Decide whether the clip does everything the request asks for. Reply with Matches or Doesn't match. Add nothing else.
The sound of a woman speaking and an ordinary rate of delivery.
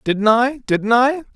Doesn't match